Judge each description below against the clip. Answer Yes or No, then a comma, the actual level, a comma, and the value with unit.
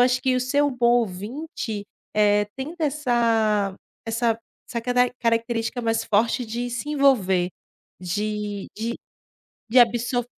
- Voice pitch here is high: Yes, high, 235 Hz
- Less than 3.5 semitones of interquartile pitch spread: Yes, average, 2.8 semitones